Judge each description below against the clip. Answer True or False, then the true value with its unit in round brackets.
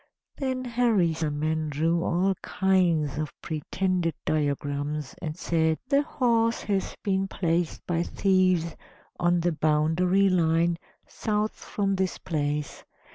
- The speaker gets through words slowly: True (115 wpm)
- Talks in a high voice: False (170 Hz)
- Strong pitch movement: False (3.6 semitones)